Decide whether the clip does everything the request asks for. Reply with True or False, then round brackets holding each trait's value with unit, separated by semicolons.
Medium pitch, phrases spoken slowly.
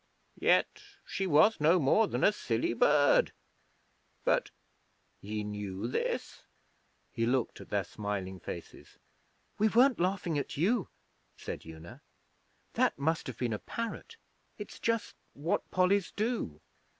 True (150 Hz; 130 wpm)